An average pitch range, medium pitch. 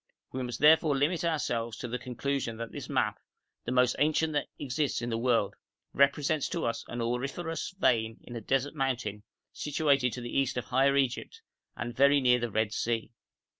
No: average, 3.3 semitones; low, 130 Hz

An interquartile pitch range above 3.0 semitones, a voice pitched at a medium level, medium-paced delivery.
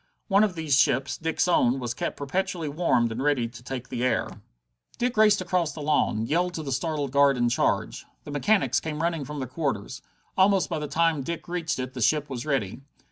No: average, 4.7 semitones; medium, 150 Hz; fast, 210 wpm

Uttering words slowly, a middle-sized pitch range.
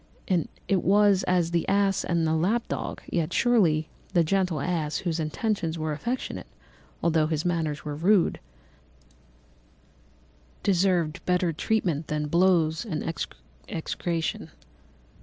Yes: slow, 120 wpm; average, 3.3 semitones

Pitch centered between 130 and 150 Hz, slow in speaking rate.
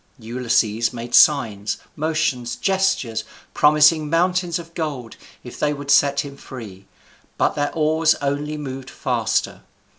Yes: medium, 140 Hz; slow, 125 wpm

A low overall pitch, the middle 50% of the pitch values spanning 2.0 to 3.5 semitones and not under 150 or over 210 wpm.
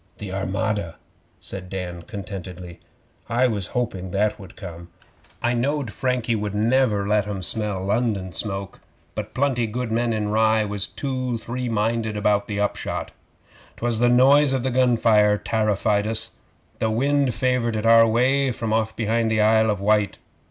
Yes: low, 110 Hz; average, 2.9 semitones; average, 165 wpm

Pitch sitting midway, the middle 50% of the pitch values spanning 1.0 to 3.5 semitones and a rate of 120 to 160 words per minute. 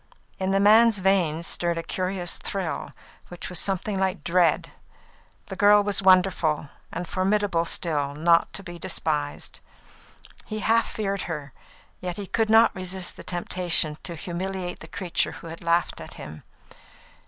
Yes: medium, 180 Hz; average, 2.7 semitones; average, 155 wpm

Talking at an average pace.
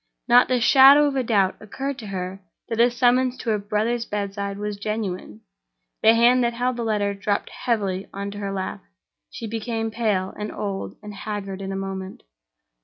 Yes: average, 180 wpm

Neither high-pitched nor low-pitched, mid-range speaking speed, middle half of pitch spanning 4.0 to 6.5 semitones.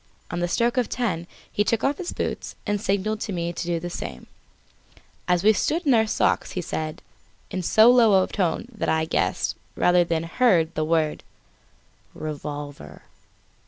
Yes: medium, 180 Hz; average, 175 wpm; average, 5.1 semitones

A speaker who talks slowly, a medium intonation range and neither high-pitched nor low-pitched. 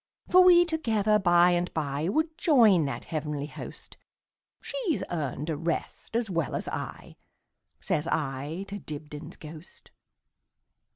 No: slow, 120 wpm; wide, 6.8 semitones; medium, 170 Hz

